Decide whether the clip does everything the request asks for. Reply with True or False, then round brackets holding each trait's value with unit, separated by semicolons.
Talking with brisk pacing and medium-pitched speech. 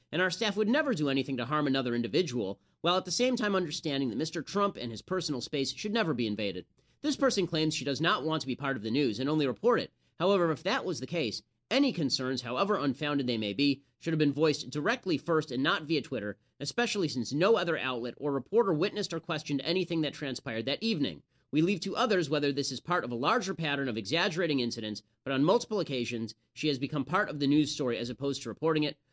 True (235 wpm; 150 Hz)